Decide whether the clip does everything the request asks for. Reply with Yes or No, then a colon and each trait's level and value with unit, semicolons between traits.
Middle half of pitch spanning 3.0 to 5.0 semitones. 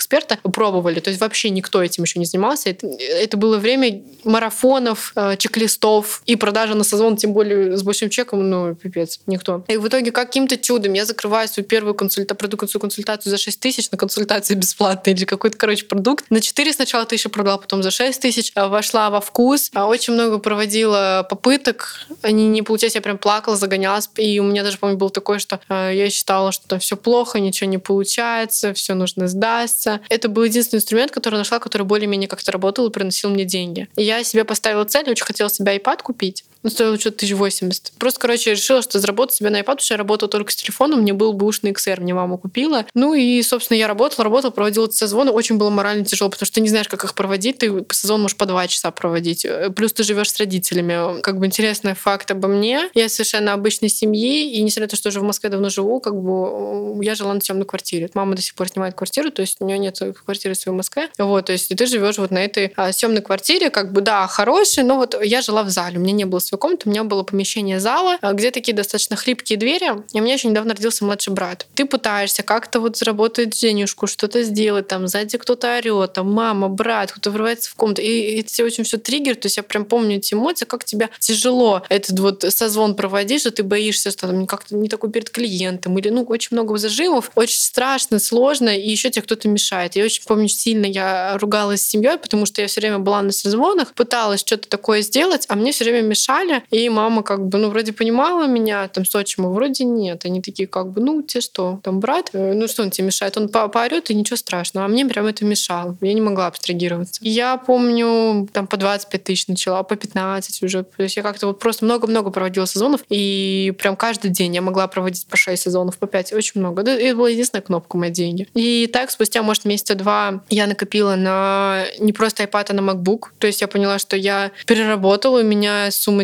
No: narrow, 2.6 semitones